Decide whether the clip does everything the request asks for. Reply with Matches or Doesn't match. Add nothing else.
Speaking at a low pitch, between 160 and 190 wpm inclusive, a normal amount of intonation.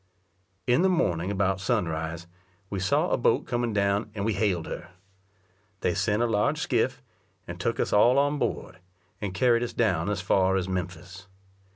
Matches